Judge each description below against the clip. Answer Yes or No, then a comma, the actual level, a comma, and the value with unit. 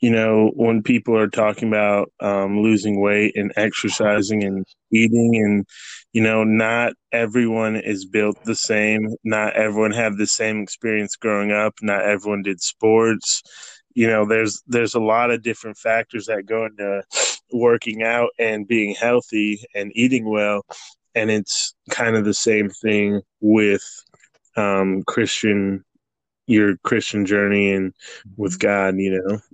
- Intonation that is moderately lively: No, narrow, 1.7 semitones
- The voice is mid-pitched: No, low, 105 Hz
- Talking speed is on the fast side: No, average, 150 wpm